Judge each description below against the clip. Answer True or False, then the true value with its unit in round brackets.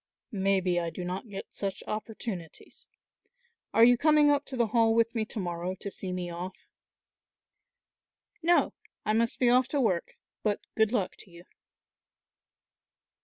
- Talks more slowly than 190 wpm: True (155 wpm)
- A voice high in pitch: True (215 Hz)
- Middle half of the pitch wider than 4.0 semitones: True (4.7 semitones)